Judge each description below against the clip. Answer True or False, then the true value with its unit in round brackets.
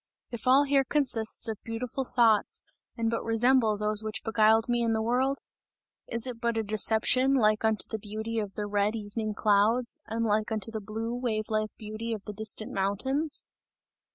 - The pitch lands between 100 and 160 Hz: False (225 Hz)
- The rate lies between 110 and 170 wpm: False (180 wpm)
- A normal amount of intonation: False (1.9 semitones)